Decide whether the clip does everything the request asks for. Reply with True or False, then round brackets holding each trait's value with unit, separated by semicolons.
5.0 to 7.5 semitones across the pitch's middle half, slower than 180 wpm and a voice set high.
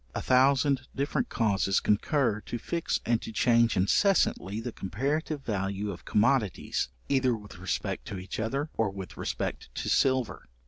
False (5.3 semitones; 150 wpm; 115 Hz)